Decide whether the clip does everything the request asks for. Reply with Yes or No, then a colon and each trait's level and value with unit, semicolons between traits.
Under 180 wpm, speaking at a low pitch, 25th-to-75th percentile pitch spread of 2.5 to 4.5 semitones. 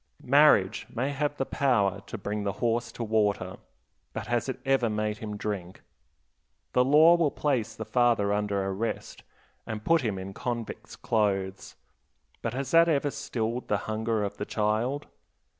Yes: average, 160 wpm; low, 110 Hz; average, 4.1 semitones